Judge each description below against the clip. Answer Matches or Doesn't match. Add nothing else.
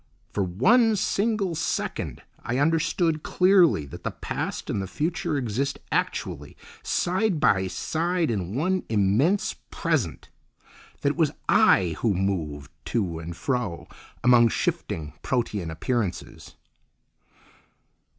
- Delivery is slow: Matches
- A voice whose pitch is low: Matches